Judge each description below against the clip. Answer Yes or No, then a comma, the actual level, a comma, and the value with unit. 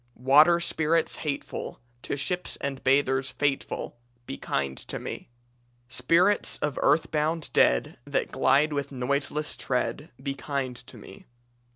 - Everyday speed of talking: No, slow, 130 wpm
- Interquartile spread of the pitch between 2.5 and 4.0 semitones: Yes, average, 2.8 semitones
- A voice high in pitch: No, medium, 140 Hz